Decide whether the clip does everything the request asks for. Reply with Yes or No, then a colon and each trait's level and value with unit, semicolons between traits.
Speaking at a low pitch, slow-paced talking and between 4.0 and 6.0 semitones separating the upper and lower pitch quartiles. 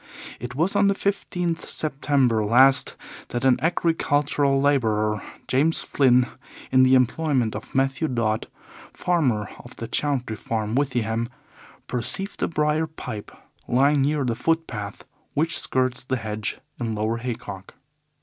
Yes: low, 130 Hz; slow, 130 wpm; average, 4.5 semitones